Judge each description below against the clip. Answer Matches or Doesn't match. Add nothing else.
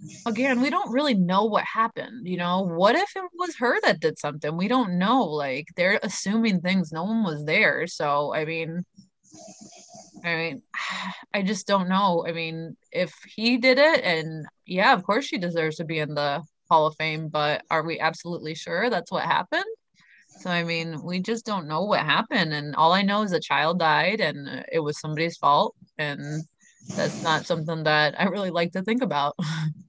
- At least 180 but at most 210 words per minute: Matches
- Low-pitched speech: Doesn't match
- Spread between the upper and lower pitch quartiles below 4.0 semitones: Doesn't match